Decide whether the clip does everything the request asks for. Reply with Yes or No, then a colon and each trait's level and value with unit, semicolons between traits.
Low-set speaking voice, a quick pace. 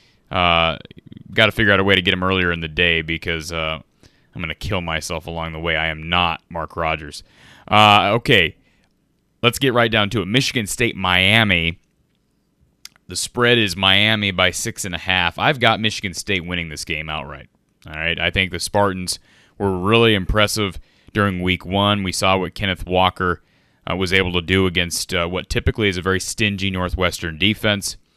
No: very low, 95 Hz; average, 185 wpm